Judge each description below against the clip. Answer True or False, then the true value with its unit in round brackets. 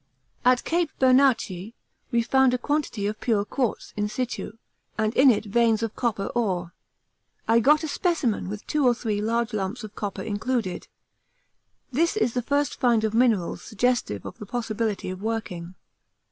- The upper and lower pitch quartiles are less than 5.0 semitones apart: True (3.4 semitones)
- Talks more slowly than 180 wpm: True (165 wpm)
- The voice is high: True (230 Hz)